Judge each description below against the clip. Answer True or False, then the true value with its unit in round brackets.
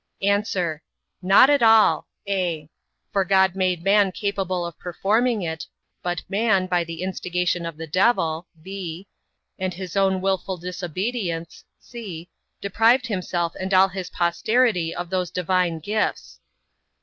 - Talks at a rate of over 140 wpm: False (135 wpm)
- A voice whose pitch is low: False (185 Hz)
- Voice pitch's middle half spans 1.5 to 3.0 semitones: True (2.5 semitones)